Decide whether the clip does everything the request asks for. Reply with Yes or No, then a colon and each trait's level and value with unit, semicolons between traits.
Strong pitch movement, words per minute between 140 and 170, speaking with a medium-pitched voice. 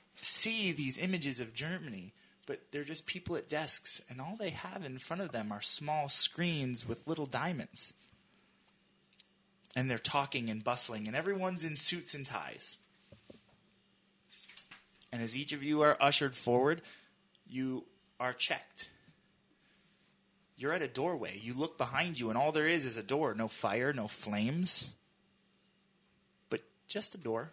Yes: wide, 6.8 semitones; average, 155 wpm; medium, 150 Hz